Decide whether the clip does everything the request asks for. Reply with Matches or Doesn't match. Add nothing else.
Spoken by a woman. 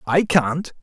Doesn't match